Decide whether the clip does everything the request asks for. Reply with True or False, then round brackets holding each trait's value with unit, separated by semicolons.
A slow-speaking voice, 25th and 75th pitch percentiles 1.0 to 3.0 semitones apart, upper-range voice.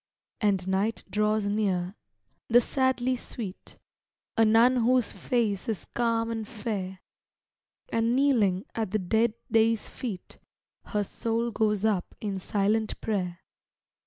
True (125 wpm; 2.5 semitones; 220 Hz)